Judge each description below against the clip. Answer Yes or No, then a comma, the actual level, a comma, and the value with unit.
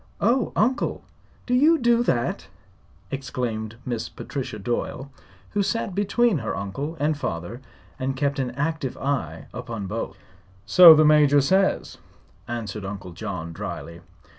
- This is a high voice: No, low, 135 Hz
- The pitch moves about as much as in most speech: No, wide, 7.7 semitones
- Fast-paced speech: No, slow, 135 wpm